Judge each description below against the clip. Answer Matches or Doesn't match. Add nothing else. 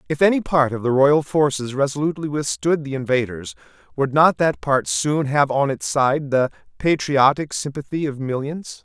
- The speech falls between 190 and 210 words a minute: Doesn't match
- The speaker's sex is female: Doesn't match